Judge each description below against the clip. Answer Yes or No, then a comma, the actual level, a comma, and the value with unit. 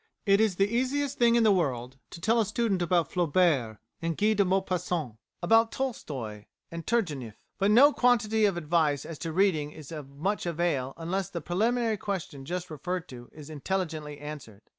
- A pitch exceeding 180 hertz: No, medium, 175 Hz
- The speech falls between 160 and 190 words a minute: Yes, average, 180 wpm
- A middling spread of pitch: No, wide, 6.0 semitones